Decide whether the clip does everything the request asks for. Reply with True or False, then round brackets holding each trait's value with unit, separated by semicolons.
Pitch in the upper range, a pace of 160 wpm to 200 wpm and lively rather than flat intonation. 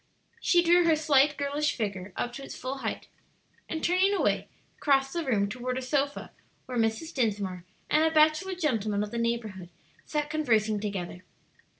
True (265 Hz; 170 wpm; 6.2 semitones)